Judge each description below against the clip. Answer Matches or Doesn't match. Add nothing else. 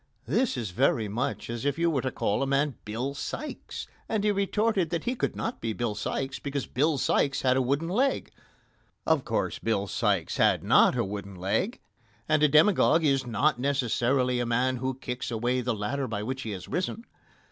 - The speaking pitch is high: Doesn't match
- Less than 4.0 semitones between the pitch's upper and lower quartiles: Doesn't match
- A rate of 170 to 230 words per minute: Matches